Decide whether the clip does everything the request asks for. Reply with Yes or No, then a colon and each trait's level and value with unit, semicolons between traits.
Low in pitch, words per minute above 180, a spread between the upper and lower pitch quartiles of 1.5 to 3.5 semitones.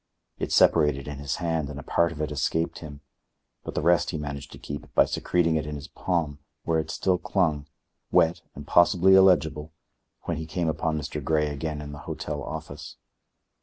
Yes: very low, 80 Hz; average, 195 wpm; narrow, 2.4 semitones